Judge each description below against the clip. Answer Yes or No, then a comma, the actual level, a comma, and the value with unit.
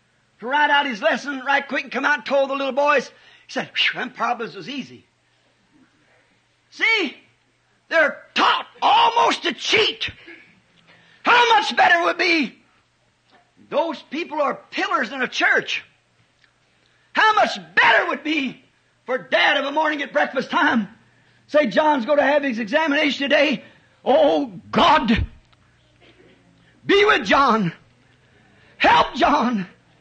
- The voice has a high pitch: Yes, very high, 285 Hz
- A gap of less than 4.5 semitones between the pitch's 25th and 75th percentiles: Yes, average, 4.1 semitones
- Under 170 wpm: Yes, slow, 135 wpm